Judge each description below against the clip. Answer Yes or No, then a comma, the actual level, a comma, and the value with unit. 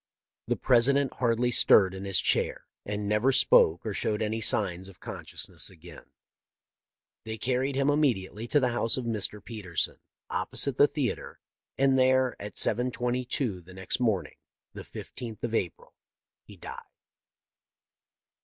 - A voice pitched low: Yes, low, 115 Hz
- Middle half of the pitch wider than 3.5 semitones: Yes, average, 4.2 semitones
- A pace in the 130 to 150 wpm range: Yes, average, 145 wpm